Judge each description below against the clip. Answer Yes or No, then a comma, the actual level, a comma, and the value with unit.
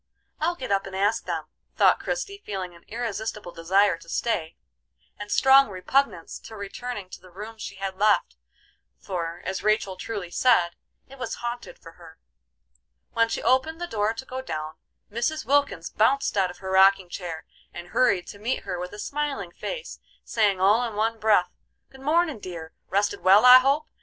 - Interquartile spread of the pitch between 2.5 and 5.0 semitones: No, wide, 5.4 semitones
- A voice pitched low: No, high, 210 Hz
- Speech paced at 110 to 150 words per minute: No, average, 180 wpm